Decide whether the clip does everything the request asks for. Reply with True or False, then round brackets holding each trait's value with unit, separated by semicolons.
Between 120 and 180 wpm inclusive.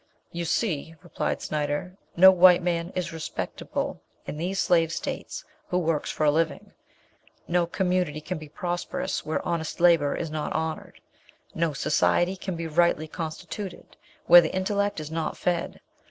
True (155 wpm)